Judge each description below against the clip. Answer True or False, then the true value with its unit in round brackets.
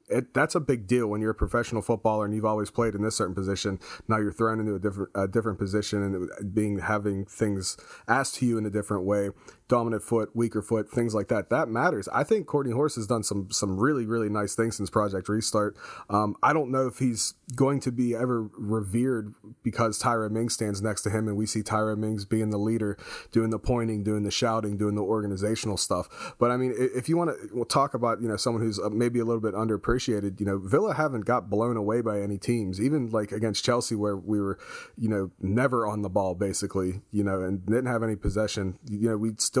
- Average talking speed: False (235 wpm)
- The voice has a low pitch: True (110 Hz)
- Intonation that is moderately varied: False (2.3 semitones)